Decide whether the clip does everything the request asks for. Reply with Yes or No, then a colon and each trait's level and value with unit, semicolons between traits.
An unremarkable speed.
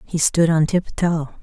Yes: average, 170 wpm